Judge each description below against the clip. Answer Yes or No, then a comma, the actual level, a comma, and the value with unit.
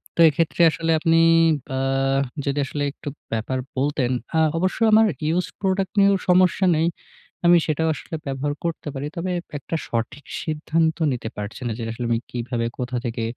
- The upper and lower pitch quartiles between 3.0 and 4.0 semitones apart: No, average, 5.1 semitones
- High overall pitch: No, medium, 150 Hz